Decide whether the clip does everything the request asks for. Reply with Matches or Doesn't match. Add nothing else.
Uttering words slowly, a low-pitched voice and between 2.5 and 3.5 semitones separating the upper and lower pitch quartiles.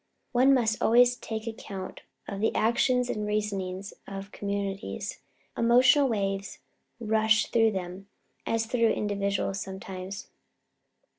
Doesn't match